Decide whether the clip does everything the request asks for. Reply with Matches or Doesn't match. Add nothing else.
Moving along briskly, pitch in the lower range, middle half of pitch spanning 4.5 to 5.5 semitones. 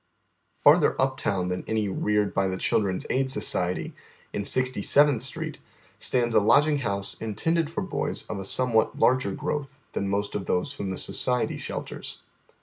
Doesn't match